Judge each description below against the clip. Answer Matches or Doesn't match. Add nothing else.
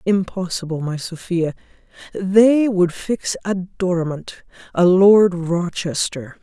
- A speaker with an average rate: Doesn't match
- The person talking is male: Doesn't match